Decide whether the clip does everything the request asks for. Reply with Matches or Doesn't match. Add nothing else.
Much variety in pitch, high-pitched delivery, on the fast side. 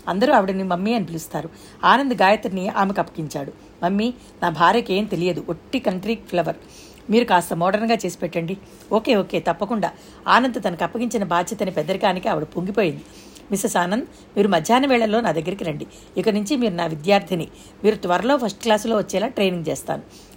Doesn't match